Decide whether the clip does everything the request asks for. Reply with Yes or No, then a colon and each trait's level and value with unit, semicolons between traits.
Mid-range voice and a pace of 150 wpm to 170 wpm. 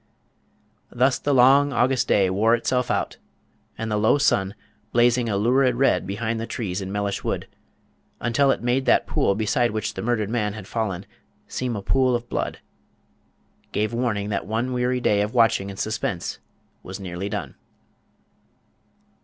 No: low, 115 Hz; average, 160 wpm